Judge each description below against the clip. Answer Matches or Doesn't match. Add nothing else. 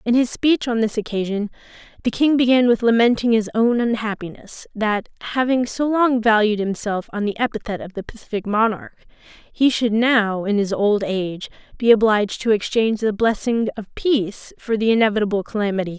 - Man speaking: Doesn't match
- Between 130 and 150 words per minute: Doesn't match